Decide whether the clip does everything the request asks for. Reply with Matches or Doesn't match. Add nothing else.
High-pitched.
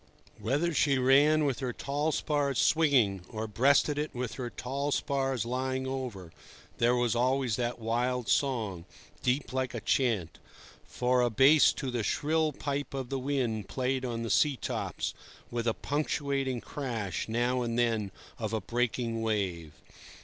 Doesn't match